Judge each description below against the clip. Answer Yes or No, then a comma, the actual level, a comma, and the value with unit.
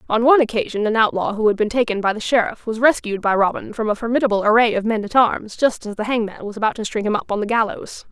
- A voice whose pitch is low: No, high, 220 Hz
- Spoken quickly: Yes, fast, 275 wpm